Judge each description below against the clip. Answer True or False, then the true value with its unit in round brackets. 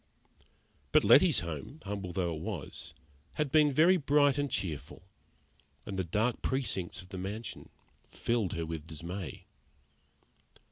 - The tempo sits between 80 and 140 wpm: True (135 wpm)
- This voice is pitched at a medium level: False (95 Hz)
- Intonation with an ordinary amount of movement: False (7.9 semitones)